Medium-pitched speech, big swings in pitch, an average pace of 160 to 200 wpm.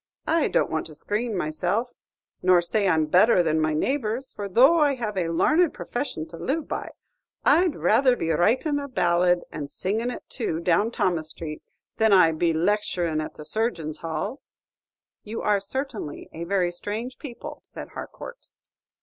No: high, 200 Hz; wide, 6.7 semitones; average, 175 wpm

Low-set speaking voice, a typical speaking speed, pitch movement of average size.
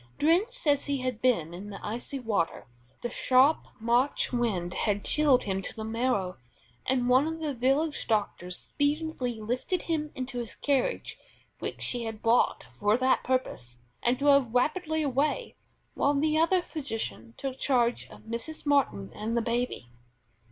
No: very high, 250 Hz; average, 160 wpm; average, 4.5 semitones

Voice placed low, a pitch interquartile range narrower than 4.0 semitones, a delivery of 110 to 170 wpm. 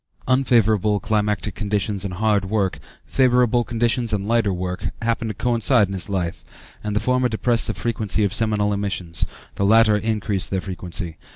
Yes: low, 105 Hz; average, 2.8 semitones; average, 165 wpm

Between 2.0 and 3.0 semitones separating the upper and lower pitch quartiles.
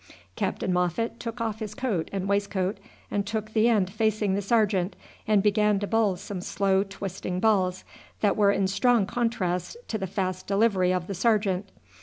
Yes: narrow, 2.5 semitones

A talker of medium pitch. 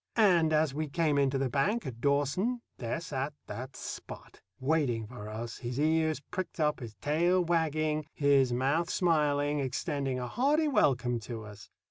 Yes: medium, 145 Hz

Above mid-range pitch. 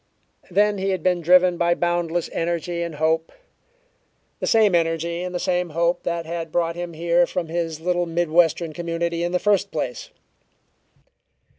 No: medium, 170 Hz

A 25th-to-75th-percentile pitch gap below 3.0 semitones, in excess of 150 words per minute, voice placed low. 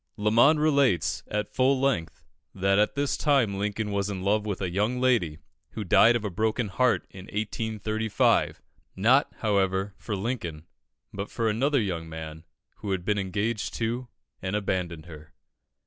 No: average, 3.6 semitones; average, 160 wpm; low, 105 Hz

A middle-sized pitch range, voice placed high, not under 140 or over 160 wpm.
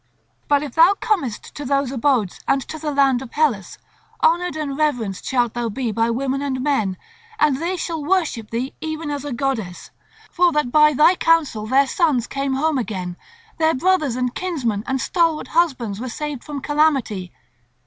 No: average, 4.3 semitones; very high, 275 Hz; average, 180 wpm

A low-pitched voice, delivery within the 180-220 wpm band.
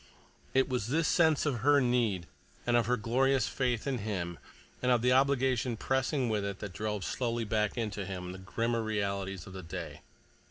Yes: low, 115 Hz; average, 190 wpm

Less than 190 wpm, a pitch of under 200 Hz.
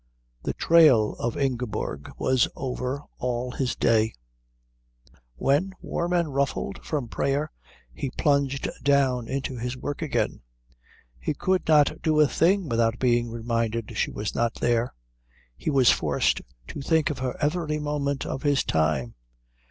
Yes: average, 145 wpm; low, 135 Hz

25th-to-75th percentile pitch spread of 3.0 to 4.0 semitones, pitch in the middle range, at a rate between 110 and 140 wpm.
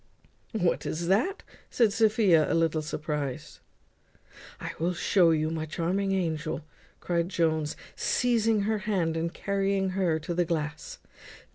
Yes: average, 3.7 semitones; medium, 175 Hz; slow, 135 wpm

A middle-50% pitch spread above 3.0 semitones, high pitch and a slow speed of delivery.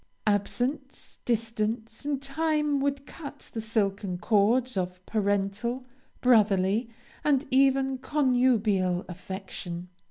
Yes: average, 5.2 semitones; high, 230 Hz; slow, 95 wpm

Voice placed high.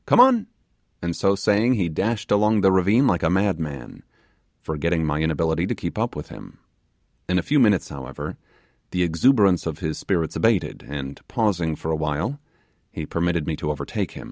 No: very low, 85 Hz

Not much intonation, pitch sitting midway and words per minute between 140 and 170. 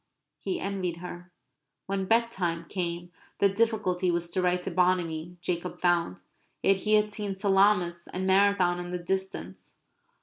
Yes: narrow, 2.1 semitones; medium, 180 Hz; average, 145 wpm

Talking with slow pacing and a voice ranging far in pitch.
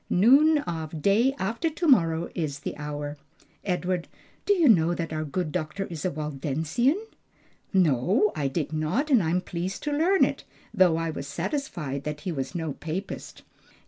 No: average, 170 wpm; wide, 5.7 semitones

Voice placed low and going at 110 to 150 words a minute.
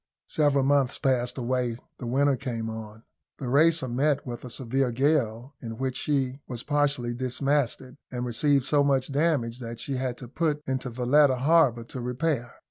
No: low, 130 Hz; average, 170 wpm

